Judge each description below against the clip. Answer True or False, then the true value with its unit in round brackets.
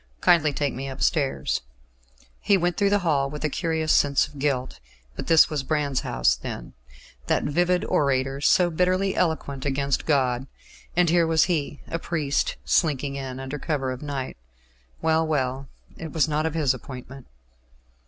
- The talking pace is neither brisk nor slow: True (160 wpm)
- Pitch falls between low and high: True (145 Hz)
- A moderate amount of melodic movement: True (3.2 semitones)